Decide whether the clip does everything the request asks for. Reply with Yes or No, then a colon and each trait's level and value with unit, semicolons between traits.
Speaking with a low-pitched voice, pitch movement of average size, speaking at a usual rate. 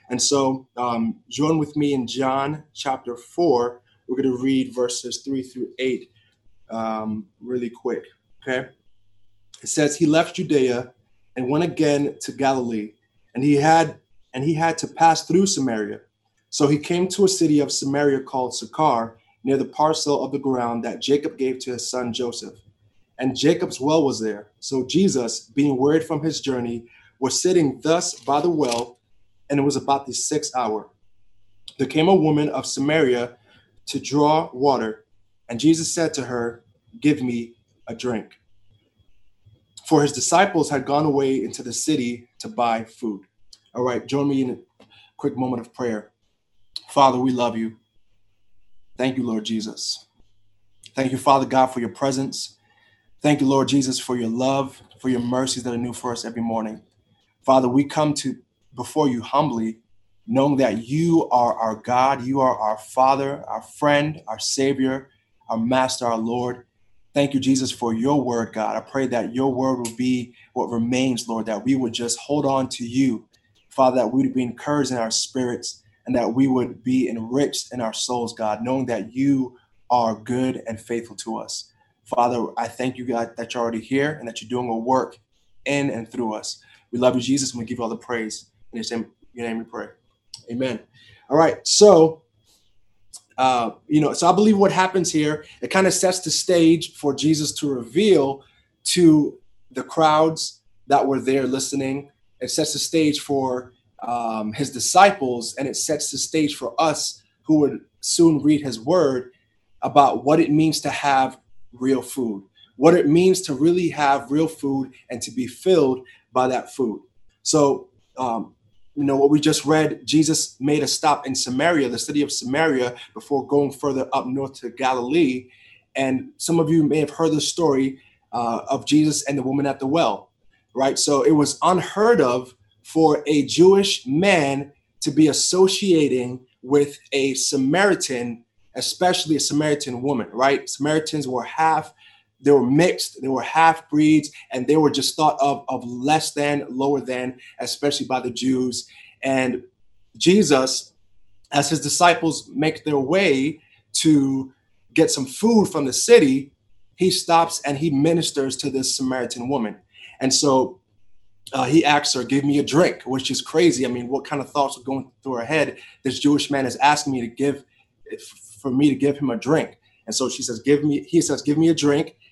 Yes: low, 130 Hz; average, 3.8 semitones; average, 180 wpm